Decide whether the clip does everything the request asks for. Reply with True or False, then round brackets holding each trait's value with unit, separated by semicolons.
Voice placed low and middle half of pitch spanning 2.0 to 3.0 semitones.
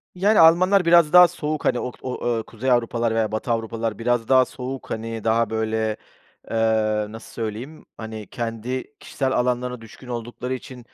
True (120 Hz; 2.7 semitones)